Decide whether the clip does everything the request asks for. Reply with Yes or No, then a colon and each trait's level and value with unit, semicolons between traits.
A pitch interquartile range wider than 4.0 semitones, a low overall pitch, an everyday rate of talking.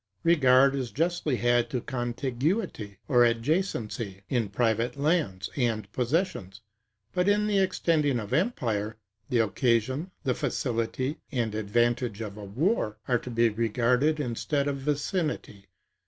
No: average, 4.7 semitones; low, 125 Hz; slow, 130 wpm